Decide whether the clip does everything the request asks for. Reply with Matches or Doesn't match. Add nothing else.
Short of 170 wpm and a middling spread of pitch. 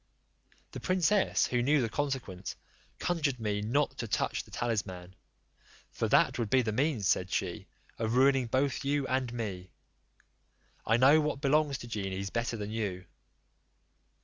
Matches